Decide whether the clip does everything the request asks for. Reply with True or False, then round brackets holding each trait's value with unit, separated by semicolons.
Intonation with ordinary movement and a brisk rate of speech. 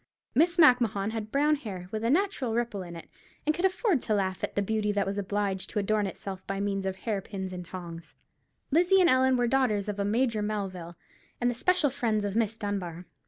True (4.7 semitones; 215 wpm)